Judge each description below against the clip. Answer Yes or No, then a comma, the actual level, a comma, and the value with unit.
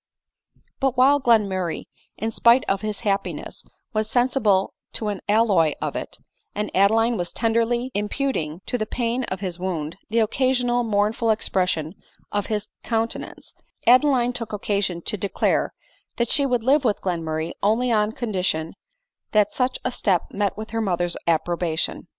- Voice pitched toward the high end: Yes, high, 215 Hz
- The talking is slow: No, average, 155 wpm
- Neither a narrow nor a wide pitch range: Yes, average, 4.2 semitones